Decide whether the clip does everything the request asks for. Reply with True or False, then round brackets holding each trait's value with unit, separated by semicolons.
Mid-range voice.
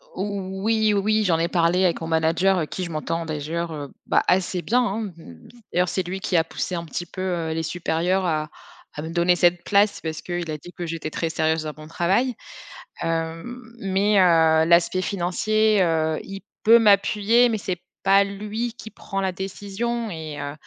True (180 Hz)